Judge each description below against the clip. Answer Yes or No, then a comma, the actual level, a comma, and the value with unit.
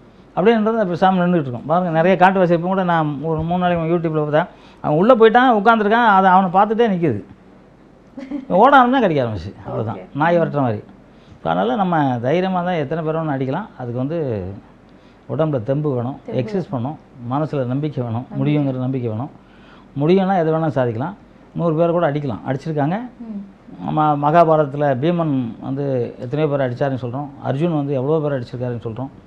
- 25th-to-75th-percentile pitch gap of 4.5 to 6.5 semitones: Yes, average, 5.1 semitones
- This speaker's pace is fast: Yes, fast, 150 wpm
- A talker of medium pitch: Yes, medium, 155 Hz